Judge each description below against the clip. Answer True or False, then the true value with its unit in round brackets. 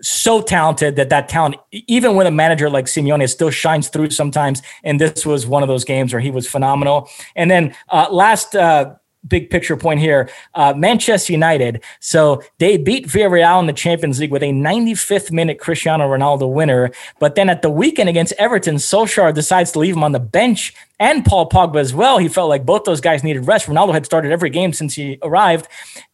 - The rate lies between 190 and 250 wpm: True (205 wpm)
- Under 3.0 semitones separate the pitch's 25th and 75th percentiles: False (3.5 semitones)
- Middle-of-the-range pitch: True (155 Hz)